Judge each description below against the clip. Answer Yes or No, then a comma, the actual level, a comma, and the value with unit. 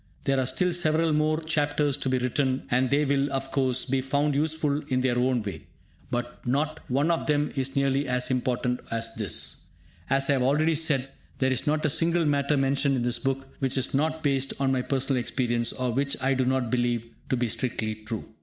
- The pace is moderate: No, fast, 210 wpm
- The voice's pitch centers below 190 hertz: Yes, low, 135 Hz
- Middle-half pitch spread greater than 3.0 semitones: No, narrow, 2.6 semitones